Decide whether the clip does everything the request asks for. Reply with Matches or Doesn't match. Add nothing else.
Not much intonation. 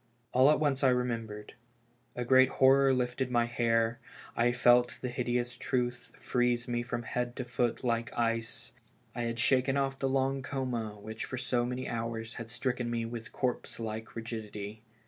Matches